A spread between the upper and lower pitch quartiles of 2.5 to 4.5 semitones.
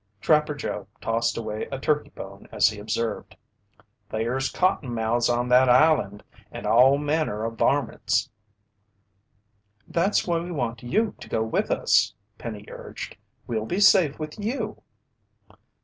No: wide, 5.6 semitones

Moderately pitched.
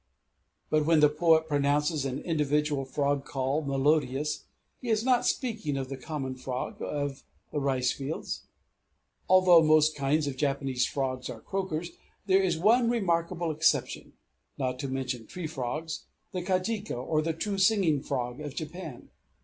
Yes: medium, 150 Hz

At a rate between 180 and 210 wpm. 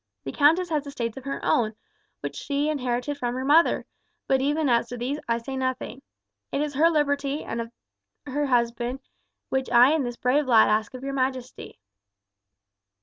Yes: average, 185 wpm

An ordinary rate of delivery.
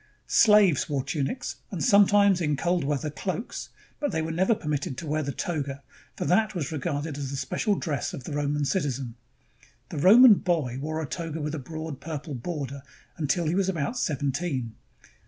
Yes: average, 180 wpm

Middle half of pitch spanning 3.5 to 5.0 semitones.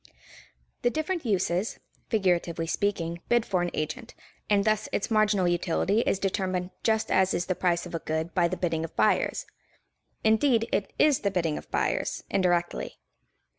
Yes: average, 3.8 semitones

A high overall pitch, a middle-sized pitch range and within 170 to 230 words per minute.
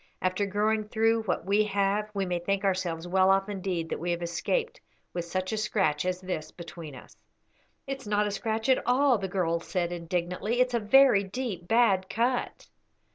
Yes: high, 195 Hz; average, 3.7 semitones; average, 185 wpm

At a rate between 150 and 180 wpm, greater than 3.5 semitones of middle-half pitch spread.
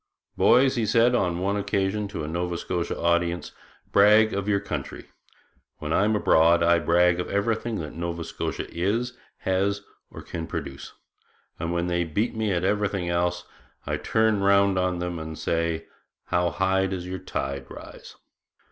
No: average, 165 wpm; average, 3.0 semitones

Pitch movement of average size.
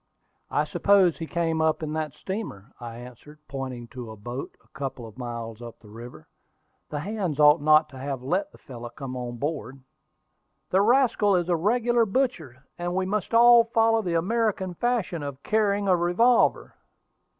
No: wide, 8.1 semitones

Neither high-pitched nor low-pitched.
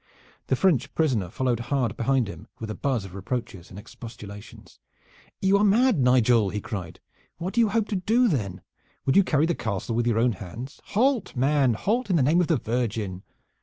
No: low, 125 Hz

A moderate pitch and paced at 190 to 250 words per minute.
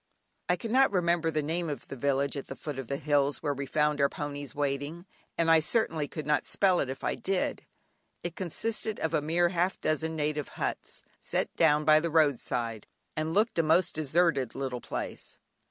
Yes: medium, 155 Hz; average, 200 wpm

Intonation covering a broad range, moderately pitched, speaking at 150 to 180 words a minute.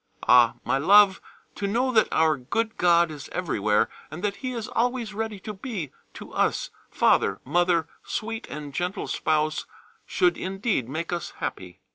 Yes: wide, 6.2 semitones; medium, 180 Hz; average, 160 wpm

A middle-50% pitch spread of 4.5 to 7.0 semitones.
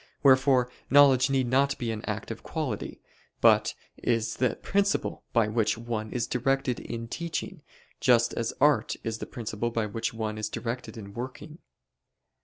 No: average, 2.8 semitones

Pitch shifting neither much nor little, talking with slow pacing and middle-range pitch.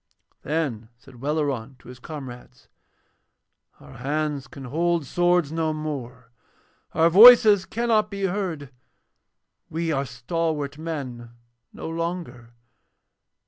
Yes: average, 4.7 semitones; slow, 105 wpm; medium, 155 Hz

